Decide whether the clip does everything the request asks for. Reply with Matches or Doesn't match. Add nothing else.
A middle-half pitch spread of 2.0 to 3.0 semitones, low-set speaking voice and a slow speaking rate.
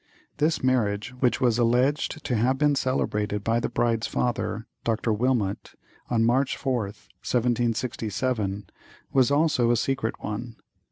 Matches